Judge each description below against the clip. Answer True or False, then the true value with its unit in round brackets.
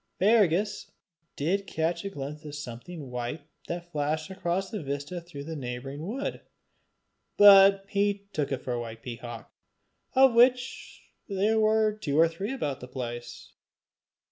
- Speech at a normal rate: True (145 wpm)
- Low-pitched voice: False (165 Hz)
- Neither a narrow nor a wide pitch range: False (6.3 semitones)